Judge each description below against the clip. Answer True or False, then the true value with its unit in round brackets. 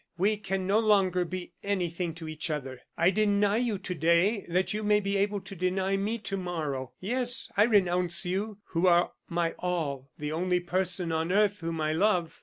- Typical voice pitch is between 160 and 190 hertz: True (185 Hz)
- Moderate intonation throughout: True (3.1 semitones)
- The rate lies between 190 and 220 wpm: True (195 wpm)